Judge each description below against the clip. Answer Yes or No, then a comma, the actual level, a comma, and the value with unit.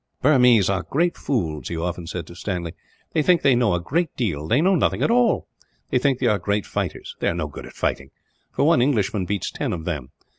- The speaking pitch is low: Yes, low, 105 Hz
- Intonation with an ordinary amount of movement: No, wide, 8.2 semitones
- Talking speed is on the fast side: Yes, fast, 230 wpm